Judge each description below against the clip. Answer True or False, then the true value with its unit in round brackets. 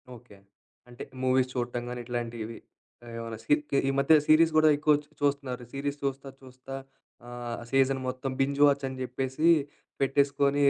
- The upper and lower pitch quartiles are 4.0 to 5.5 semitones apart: False (2.4 semitones)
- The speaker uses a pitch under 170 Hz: True (135 Hz)